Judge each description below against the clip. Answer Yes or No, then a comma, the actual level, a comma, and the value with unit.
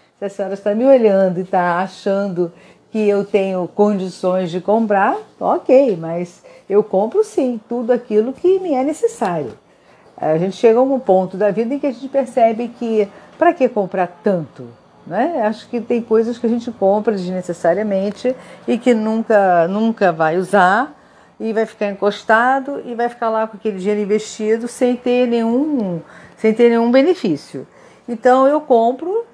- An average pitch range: Yes, average, 4.0 semitones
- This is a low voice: No, high, 220 Hz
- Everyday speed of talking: Yes, average, 165 wpm